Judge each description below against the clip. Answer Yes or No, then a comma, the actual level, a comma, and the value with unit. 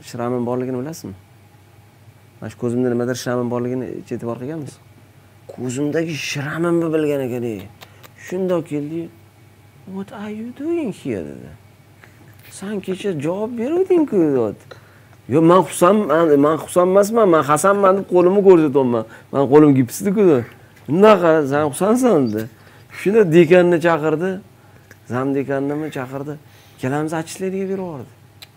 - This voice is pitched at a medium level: Yes, medium, 145 Hz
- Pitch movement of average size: No, wide, 7.0 semitones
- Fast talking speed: No, average, 115 wpm